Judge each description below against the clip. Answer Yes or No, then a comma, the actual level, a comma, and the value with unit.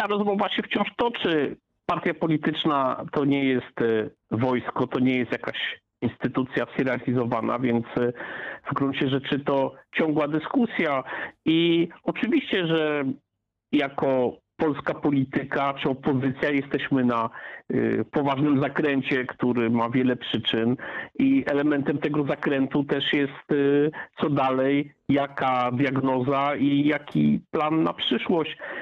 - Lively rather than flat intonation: No, average, 2.8 semitones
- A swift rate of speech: No, average, 120 wpm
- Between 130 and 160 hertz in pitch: Yes, medium, 140 Hz